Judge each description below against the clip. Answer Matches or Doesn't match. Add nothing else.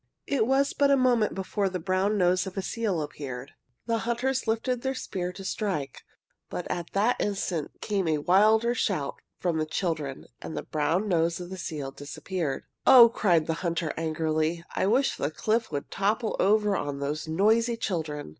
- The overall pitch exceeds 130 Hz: Matches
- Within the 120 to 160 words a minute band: Doesn't match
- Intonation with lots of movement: Matches